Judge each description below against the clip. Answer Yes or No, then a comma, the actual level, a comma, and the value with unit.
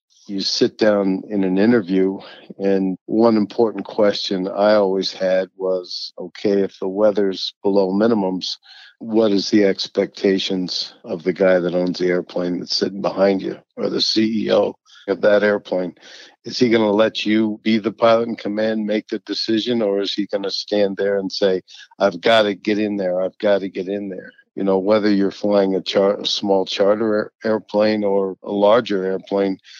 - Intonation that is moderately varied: No, narrow, 2.1 semitones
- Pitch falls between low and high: No, low, 100 Hz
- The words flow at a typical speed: Yes, average, 185 wpm